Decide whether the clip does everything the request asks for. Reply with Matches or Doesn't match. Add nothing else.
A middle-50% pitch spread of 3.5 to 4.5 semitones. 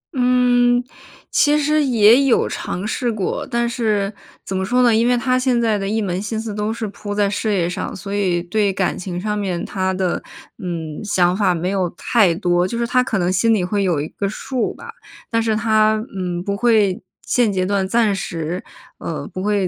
Matches